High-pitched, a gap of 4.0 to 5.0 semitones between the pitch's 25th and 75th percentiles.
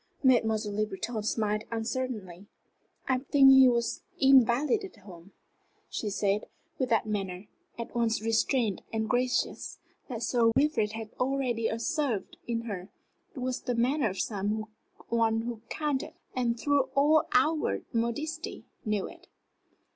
No: high, 235 Hz; average, 3.5 semitones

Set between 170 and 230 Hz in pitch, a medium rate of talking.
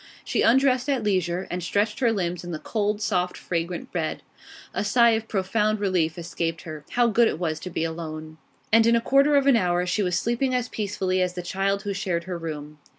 No: high, 190 Hz; fast, 215 wpm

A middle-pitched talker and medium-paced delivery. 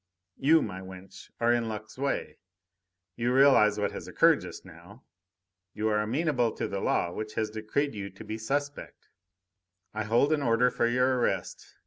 No: low, 115 Hz; average, 170 wpm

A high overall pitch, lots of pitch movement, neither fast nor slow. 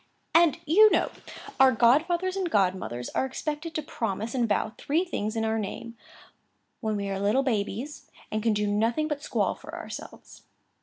Yes: high, 235 Hz; wide, 6.6 semitones; average, 170 wpm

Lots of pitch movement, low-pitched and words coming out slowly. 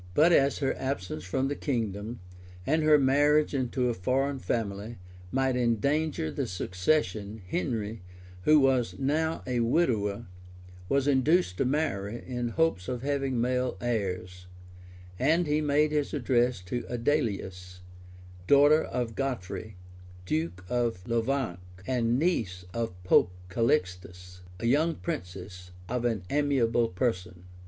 Yes: wide, 6.1 semitones; low, 120 Hz; slow, 130 wpm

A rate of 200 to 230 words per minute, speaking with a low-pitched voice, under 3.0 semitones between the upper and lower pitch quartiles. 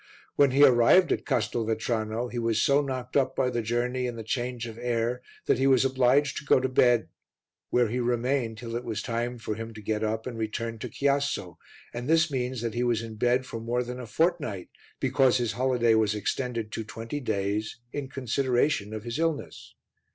Yes: fast, 205 wpm; low, 120 Hz; narrow, 2.5 semitones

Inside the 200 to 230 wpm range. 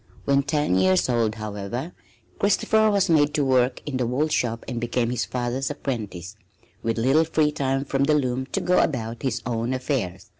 No: average, 185 wpm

